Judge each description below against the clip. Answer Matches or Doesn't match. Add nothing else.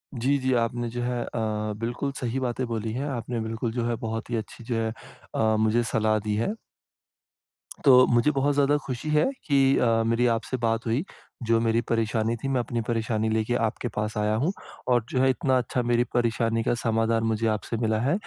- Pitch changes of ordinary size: Doesn't match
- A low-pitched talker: Matches